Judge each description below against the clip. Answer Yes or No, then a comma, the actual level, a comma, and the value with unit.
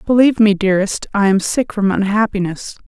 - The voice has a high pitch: Yes, high, 205 Hz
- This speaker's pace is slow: No, average, 165 wpm